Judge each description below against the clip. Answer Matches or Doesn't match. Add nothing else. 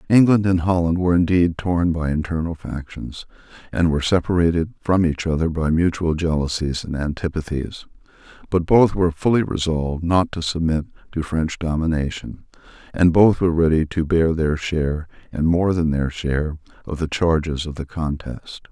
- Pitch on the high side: Doesn't match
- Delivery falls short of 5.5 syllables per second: Matches